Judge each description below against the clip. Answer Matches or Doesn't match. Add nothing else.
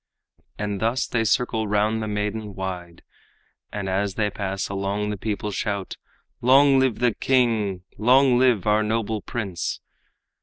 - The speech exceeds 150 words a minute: Doesn't match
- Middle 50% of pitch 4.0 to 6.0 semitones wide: Doesn't match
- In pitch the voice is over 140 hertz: Doesn't match